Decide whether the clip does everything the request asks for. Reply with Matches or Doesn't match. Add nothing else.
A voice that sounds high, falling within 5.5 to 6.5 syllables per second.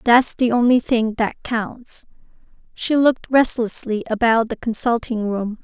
Doesn't match